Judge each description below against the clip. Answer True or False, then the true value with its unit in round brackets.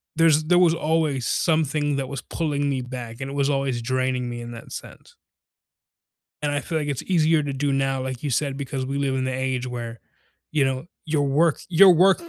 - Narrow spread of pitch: False (3.0 semitones)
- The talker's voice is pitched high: False (140 Hz)